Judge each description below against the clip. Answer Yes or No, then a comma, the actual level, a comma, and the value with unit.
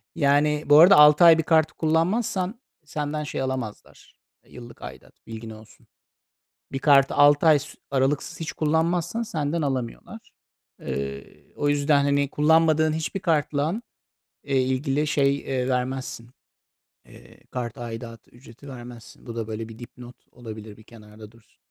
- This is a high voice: No, medium, 140 Hz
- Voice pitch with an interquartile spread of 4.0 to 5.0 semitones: Yes, average, 4.4 semitones